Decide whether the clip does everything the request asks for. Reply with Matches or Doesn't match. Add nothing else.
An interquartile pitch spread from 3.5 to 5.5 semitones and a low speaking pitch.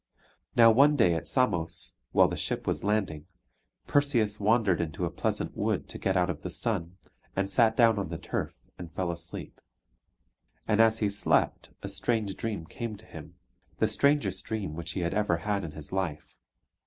Matches